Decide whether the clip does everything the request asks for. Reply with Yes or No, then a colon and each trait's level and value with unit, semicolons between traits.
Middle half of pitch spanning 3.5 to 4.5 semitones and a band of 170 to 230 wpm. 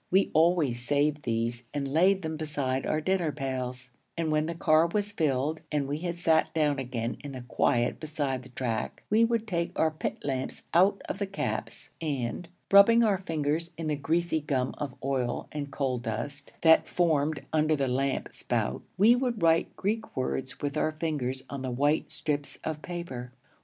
Yes: average, 4.1 semitones; average, 185 wpm